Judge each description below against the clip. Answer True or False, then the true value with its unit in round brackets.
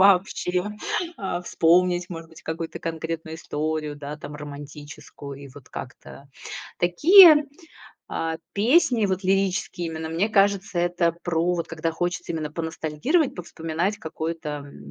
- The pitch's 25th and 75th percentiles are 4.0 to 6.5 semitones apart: False (2.9 semitones)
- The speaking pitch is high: False (165 Hz)